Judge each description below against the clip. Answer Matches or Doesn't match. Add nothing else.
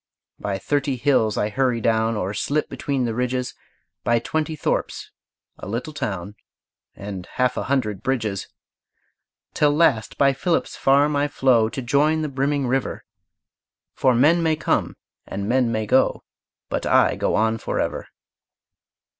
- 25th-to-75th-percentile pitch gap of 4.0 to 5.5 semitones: Matches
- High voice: Doesn't match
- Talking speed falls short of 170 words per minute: Matches